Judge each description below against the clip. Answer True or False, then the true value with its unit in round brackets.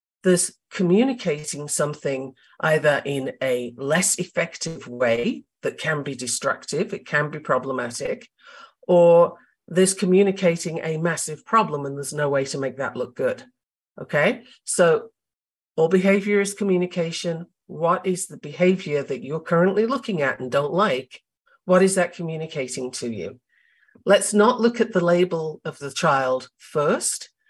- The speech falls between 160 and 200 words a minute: False (145 wpm)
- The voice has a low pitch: False (170 Hz)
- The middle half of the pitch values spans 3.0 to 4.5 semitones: False (5.1 semitones)